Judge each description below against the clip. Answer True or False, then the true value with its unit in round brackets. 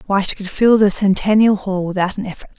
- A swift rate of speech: True (230 wpm)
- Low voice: False (200 Hz)